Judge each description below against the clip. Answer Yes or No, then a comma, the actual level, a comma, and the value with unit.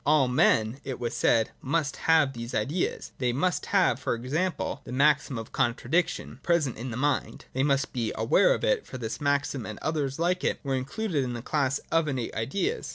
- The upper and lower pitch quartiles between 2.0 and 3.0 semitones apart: No, average, 4.2 semitones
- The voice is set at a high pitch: No, low, 135 Hz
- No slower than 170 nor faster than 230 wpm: Yes, fast, 205 wpm